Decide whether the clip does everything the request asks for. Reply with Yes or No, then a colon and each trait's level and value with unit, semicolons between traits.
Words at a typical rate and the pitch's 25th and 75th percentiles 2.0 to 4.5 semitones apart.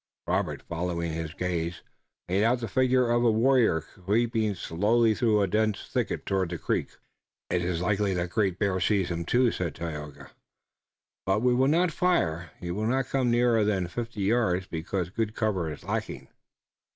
No: average, 175 wpm; average, 5.2 semitones